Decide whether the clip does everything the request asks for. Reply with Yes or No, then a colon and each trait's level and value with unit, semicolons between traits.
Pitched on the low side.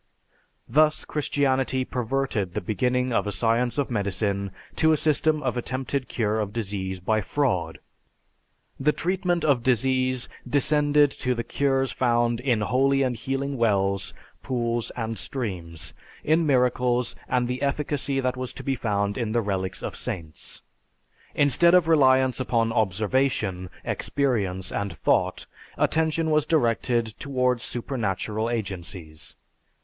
Yes: low, 125 Hz